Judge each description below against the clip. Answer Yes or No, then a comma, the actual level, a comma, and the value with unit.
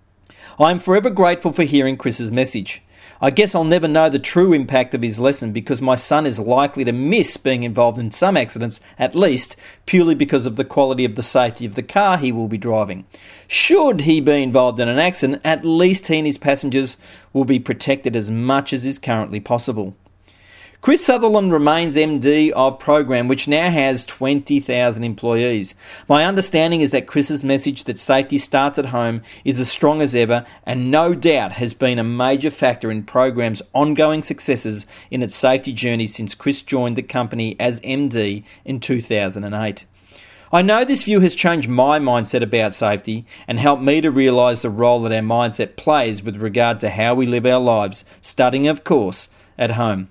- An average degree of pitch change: Yes, average, 4.1 semitones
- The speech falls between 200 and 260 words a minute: No, average, 185 wpm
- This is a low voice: Yes, low, 130 Hz